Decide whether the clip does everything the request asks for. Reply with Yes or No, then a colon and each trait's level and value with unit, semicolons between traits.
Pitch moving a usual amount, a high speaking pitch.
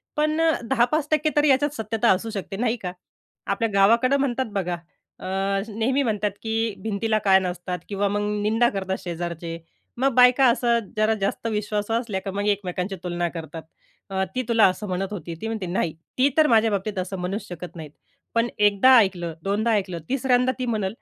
Yes: average, 4.0 semitones; high, 210 Hz